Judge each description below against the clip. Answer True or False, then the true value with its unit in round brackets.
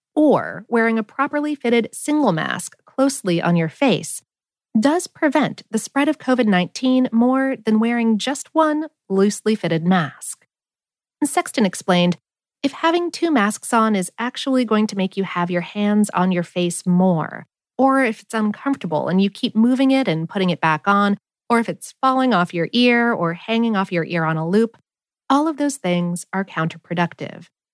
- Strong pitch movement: True (6.8 semitones)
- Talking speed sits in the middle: True (175 wpm)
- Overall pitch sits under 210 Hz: False (220 Hz)